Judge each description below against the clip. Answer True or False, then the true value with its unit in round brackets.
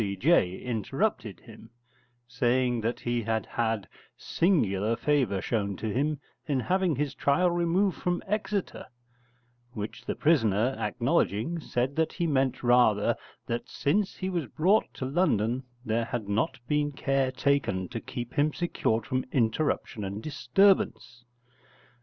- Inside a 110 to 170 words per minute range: True (135 wpm)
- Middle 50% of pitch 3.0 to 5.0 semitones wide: False (5.6 semitones)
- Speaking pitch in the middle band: False (130 Hz)